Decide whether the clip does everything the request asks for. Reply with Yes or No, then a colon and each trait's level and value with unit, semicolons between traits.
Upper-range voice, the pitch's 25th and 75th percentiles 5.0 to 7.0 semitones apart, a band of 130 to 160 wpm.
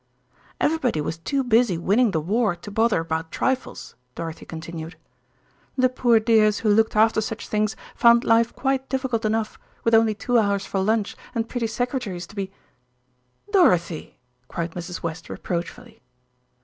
Yes: high, 215 Hz; average, 5.3 semitones; average, 155 wpm